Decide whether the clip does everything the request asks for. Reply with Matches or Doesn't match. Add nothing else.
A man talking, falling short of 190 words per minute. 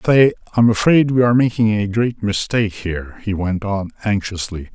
Matches